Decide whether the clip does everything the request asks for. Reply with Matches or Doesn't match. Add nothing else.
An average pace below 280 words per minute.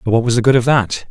Doesn't match